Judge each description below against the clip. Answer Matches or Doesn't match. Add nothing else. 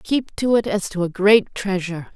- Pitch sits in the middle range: Doesn't match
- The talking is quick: Matches